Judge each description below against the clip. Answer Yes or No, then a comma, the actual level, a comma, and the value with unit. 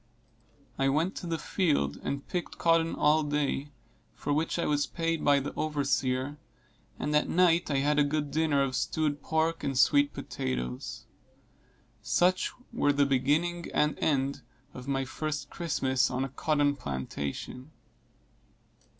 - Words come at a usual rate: Yes, average, 145 wpm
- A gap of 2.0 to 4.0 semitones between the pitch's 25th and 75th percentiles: Yes, average, 2.7 semitones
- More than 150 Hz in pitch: No, medium, 145 Hz